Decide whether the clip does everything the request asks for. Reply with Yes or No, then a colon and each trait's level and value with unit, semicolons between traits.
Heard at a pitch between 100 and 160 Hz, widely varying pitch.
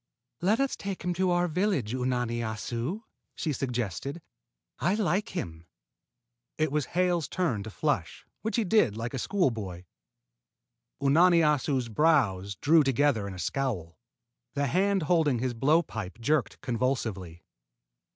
Yes: low, 135 Hz; wide, 7.4 semitones